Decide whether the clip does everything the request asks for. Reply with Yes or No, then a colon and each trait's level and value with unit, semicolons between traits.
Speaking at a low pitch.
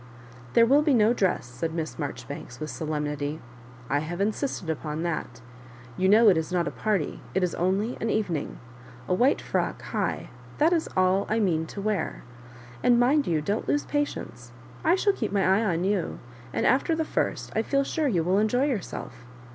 No: high, 195 Hz